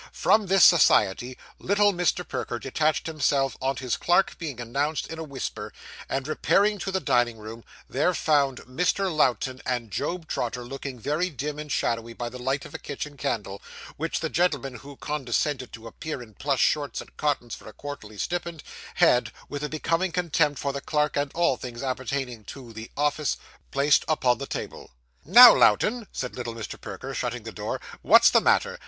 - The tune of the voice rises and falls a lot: No, average, 4.3 semitones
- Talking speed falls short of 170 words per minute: No, average, 185 wpm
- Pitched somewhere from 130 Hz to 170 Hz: Yes, medium, 140 Hz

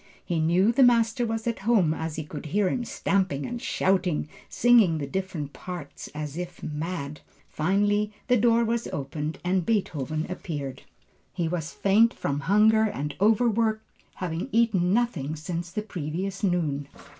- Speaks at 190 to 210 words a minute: No, average, 155 wpm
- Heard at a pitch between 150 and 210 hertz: Yes, medium, 185 Hz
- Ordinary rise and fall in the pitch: No, wide, 5.8 semitones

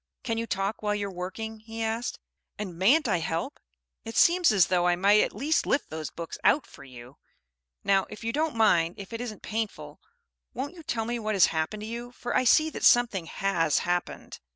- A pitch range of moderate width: Yes, average, 4.7 semitones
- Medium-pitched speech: No, high, 215 Hz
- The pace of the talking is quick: Yes, fast, 210 wpm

